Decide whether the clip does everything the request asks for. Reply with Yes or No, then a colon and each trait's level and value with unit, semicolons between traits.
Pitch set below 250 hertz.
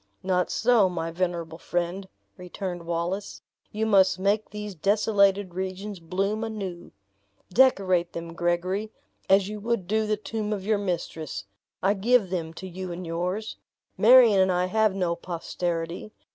Yes: high, 190 Hz